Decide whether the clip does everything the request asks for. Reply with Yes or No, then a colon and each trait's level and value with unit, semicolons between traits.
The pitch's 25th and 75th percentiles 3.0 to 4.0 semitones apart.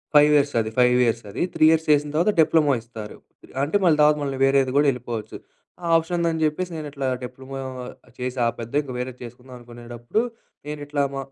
Yes: average, 3.5 semitones